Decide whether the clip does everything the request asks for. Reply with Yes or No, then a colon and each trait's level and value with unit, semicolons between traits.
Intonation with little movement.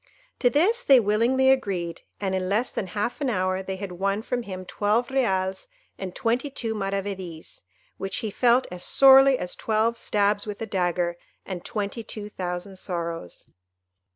No: average, 4.0 semitones